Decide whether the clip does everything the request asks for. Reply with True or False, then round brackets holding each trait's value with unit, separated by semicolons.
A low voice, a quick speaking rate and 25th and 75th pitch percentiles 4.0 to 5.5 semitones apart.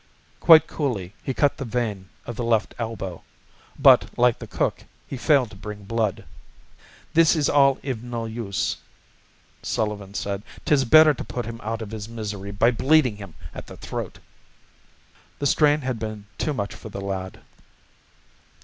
False (115 Hz; 165 wpm; 4.6 semitones)